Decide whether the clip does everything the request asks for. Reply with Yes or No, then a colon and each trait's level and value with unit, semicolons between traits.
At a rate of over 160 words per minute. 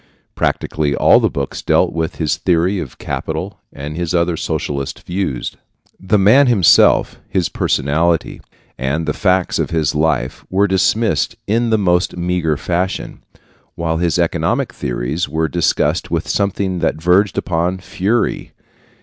No: average, 140 wpm